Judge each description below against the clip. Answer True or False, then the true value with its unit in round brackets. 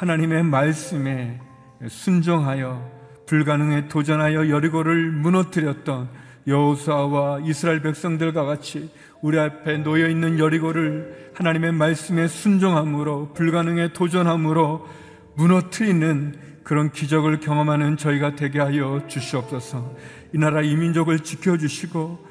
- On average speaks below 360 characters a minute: True (305 characters per minute)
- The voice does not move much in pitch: True (2.0 semitones)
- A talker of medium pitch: True (155 Hz)